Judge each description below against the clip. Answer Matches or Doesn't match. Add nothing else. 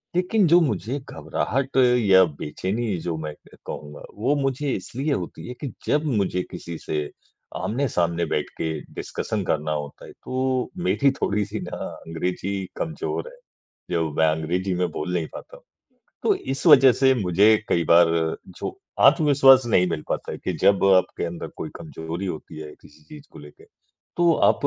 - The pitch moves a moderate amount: Doesn't match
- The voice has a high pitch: Doesn't match